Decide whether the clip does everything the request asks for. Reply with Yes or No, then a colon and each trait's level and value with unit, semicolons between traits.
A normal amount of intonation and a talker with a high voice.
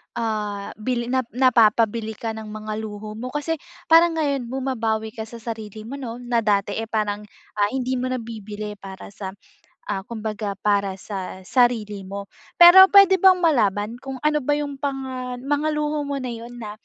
Yes: average, 4.1 semitones; high, 230 Hz